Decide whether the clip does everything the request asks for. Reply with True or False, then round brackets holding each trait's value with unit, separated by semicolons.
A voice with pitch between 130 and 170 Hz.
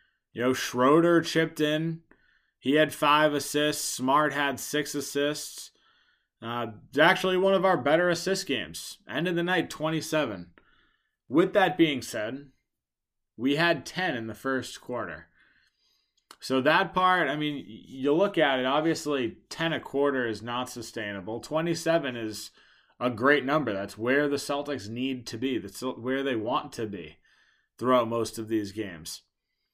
True (140 Hz)